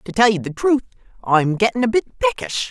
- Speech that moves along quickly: Yes, fast, 220 wpm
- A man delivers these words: No, female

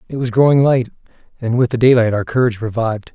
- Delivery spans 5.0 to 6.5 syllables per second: No, 6.9 syllables/s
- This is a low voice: Yes, low, 120 Hz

